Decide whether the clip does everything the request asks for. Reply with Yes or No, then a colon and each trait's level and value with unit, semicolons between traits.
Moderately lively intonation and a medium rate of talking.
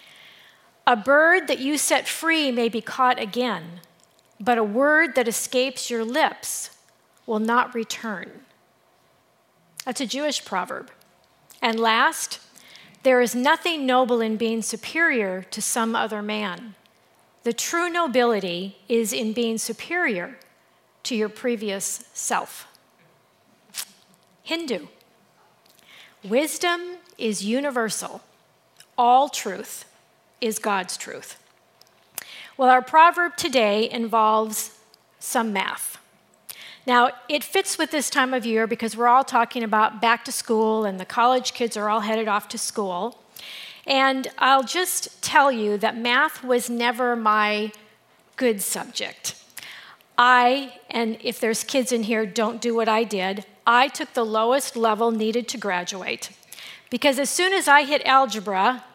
No: average, 3.3 semitones; slow, 130 wpm